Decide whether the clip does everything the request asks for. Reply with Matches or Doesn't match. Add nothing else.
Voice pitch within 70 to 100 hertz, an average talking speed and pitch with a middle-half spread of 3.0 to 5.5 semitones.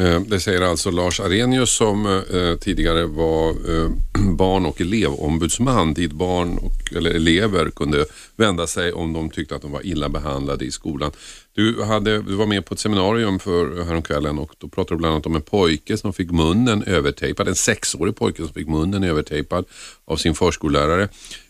Matches